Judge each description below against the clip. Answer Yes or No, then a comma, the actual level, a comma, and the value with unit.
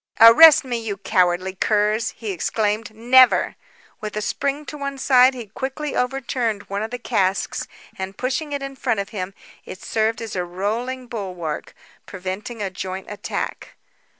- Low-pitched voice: No, high, 220 Hz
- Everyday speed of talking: Yes, average, 160 wpm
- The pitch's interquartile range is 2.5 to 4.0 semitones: No, average, 4.6 semitones